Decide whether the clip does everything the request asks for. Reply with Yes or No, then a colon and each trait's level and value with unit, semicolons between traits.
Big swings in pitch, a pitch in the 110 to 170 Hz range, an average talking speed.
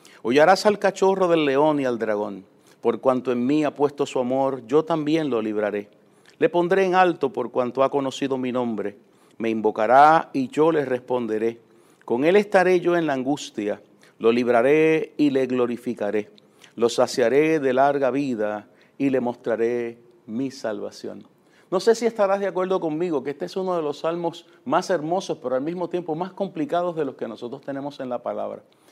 Yes: wide, 5.9 semitones; medium, 140 Hz; average, 185 wpm